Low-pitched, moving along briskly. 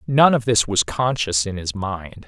Yes: low, 105 Hz; fast, 210 wpm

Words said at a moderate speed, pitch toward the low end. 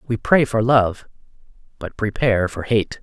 Yes: average, 160 wpm; low, 115 Hz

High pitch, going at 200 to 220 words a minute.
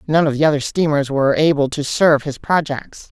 No: medium, 145 Hz; fast, 205 wpm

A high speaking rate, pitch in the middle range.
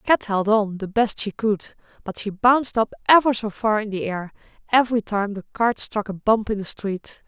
No: fast, 225 wpm; high, 215 Hz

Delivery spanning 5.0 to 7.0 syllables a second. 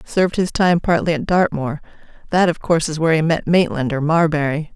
Yes: 5.8 syllables/s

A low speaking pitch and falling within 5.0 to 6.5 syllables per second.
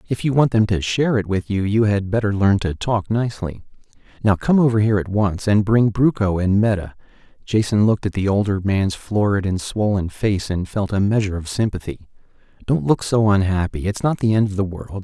Yes: low, 100 Hz; 5.5 syllables/s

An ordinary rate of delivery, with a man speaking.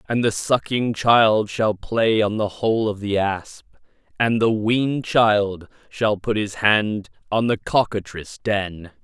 Yes: average, 160 wpm; male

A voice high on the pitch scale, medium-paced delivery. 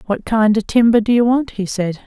No: high, 220 Hz; fast, 260 wpm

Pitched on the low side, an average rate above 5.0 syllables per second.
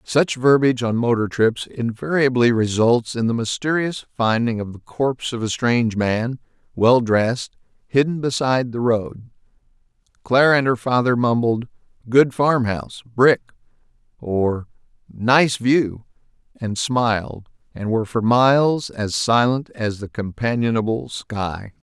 No: low, 120 Hz; 4.4 syllables/s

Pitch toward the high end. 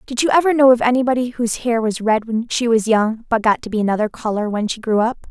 Yes: high, 230 Hz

